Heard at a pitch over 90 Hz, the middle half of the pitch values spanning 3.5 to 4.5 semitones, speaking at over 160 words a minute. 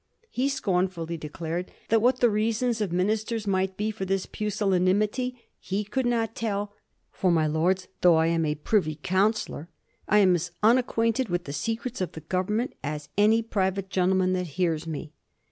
Yes: high, 190 Hz; average, 4.0 semitones; average, 180 wpm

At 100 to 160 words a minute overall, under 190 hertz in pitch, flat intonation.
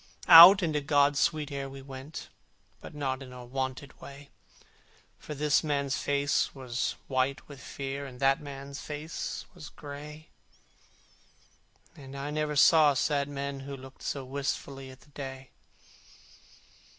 Yes: average, 140 wpm; medium, 140 Hz; narrow, 1.5 semitones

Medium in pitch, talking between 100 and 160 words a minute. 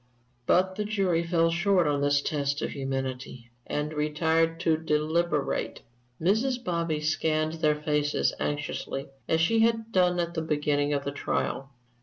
Yes: medium, 155 Hz; average, 150 wpm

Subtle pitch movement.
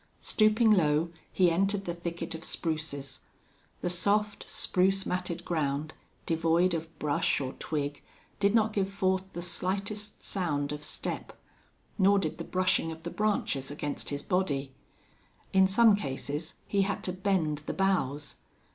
No: average, 4.3 semitones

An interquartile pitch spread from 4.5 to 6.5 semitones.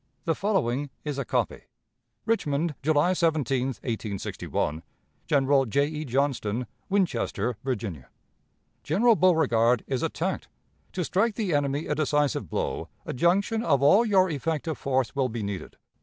Yes: average, 5.3 semitones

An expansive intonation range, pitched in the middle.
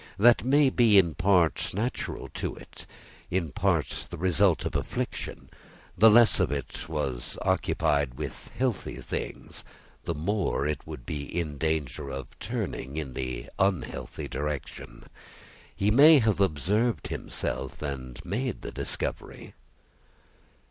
No: wide, 6.9 semitones; very low, 80 Hz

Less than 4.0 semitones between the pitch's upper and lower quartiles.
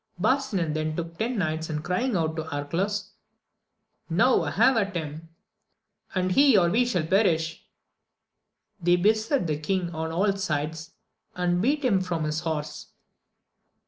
No: average, 4.4 semitones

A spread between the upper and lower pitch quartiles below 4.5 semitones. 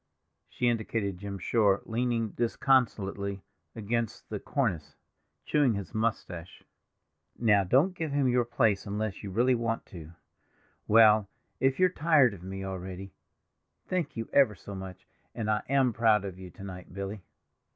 Yes: average, 3.8 semitones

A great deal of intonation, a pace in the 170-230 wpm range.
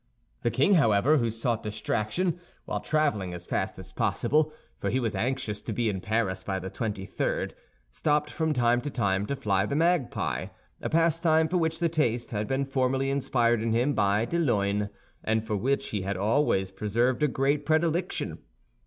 Yes: wide, 6.2 semitones; average, 180 wpm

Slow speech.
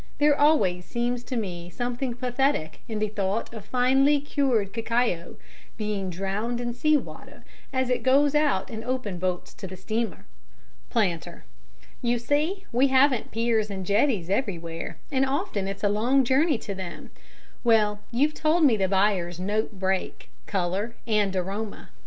No: average, 155 wpm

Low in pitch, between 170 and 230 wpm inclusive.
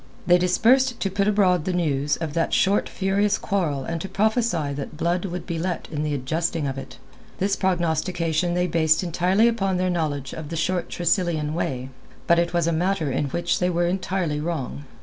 No: medium, 175 Hz; average, 200 wpm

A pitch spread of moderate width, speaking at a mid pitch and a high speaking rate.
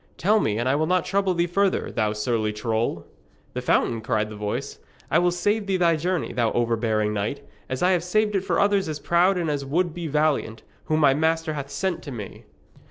No: wide, 7.7 semitones; medium, 155 Hz; fast, 220 wpm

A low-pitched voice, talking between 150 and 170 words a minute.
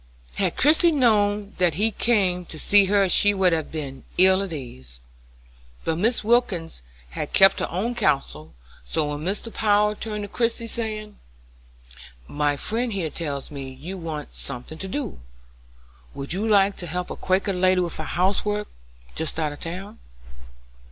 No: medium, 185 Hz; average, 165 wpm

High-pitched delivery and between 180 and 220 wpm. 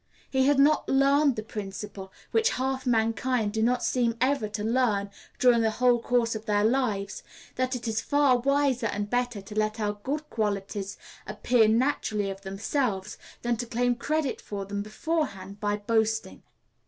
No: high, 230 Hz; average, 165 wpm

